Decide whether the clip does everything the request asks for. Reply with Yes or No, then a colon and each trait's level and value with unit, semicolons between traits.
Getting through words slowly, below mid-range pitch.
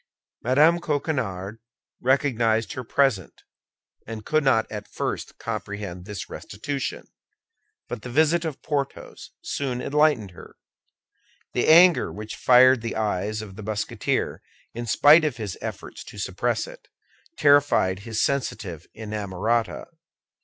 Yes: slow, 125 wpm; low, 120 Hz